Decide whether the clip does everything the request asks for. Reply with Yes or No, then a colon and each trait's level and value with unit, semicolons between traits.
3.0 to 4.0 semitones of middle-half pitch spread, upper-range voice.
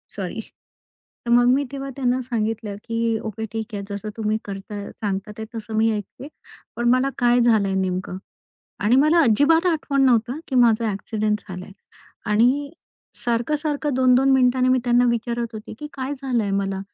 Yes: average, 3.4 semitones; high, 235 Hz